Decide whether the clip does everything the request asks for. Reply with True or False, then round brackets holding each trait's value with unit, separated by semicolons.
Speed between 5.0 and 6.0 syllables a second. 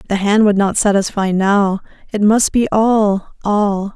False (3.9 syllables/s)